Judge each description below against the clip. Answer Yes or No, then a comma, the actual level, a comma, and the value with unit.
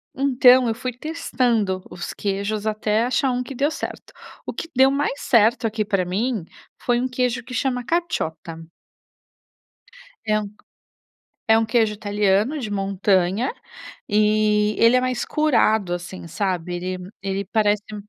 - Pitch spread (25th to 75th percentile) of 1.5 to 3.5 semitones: No, average, 4.1 semitones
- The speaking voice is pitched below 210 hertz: No, high, 215 Hz